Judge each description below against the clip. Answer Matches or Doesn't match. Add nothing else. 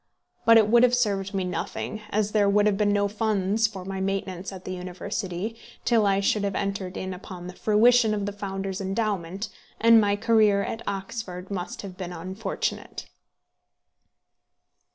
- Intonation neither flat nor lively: Doesn't match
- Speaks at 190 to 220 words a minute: Doesn't match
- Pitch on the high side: Matches